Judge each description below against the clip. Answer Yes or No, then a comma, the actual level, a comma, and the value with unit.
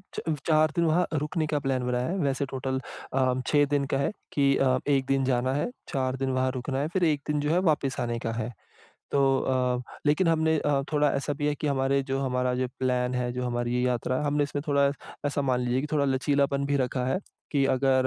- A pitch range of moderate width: No, narrow, 2.3 semitones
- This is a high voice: No, low, 135 Hz